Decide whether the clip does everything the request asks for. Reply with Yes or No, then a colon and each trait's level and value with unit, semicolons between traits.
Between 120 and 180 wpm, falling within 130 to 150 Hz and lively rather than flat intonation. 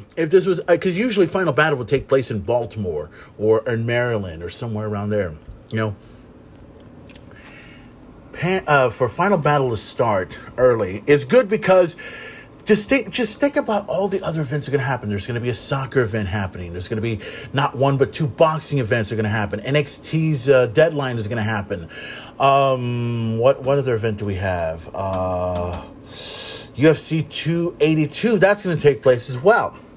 No: average, 190 wpm; low, 135 Hz; wide, 6.2 semitones